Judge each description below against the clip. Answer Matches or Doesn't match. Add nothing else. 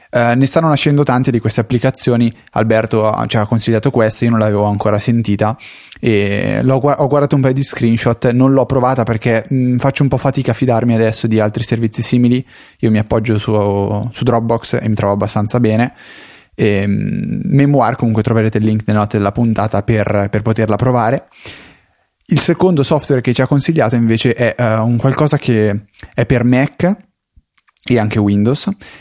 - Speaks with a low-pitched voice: Matches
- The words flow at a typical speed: Doesn't match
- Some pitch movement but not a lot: Matches